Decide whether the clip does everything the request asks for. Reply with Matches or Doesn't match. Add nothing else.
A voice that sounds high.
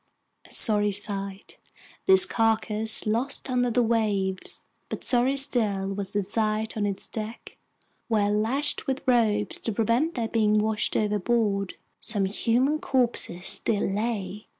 Matches